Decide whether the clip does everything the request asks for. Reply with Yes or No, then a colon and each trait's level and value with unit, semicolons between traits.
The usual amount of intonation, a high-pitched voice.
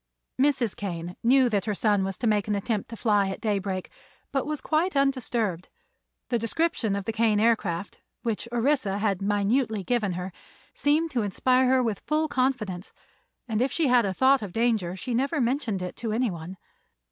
Yes: average, 4.5 semitones; high, 225 Hz